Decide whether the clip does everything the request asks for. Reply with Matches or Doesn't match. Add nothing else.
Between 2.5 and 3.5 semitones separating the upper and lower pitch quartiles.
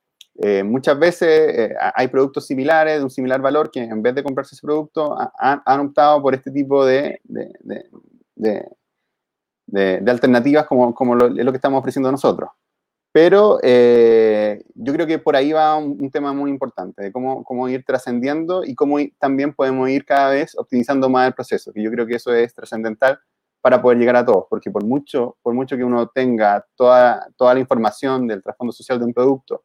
Matches